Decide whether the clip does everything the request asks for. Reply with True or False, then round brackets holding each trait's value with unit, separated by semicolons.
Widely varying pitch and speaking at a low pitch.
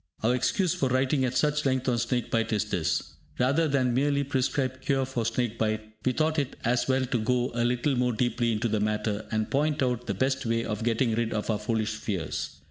False (2.9 semitones; 125 Hz)